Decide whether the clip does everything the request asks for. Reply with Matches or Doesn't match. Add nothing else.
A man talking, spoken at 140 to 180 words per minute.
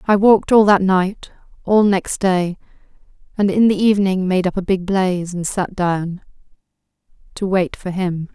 Doesn't match